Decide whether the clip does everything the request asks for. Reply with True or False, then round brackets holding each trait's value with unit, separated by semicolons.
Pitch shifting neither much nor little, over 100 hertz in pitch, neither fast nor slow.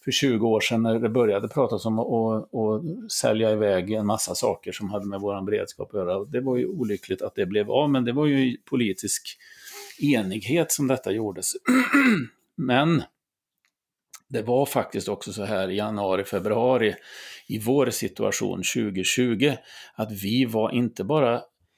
True (4.0 semitones; 115 Hz; 165 wpm)